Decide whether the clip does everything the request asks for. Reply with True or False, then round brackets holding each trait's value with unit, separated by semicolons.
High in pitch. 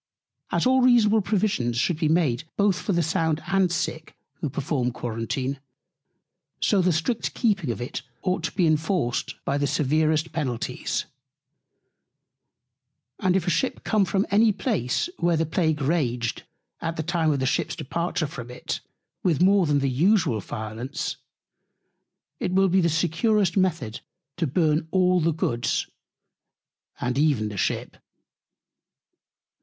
False (160 Hz)